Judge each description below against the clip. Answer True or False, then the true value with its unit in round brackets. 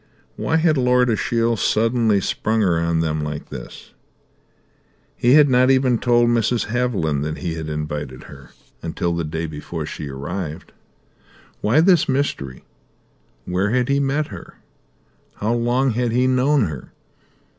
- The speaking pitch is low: True (110 Hz)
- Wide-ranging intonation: True (7.8 semitones)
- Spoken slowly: False (145 wpm)